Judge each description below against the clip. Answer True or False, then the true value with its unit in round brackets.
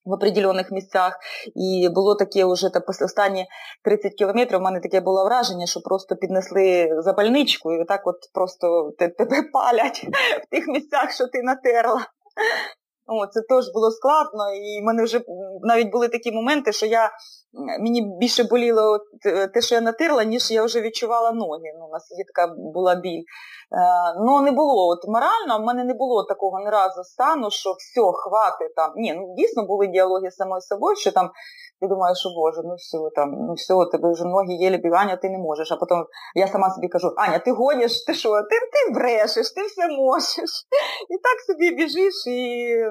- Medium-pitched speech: False (210 Hz)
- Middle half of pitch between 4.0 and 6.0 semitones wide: True (4.7 semitones)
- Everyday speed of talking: False (185 wpm)